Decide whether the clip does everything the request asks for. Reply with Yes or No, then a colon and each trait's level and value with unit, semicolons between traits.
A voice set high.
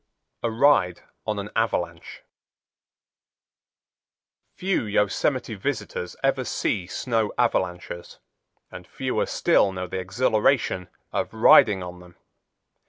No: low, 105 Hz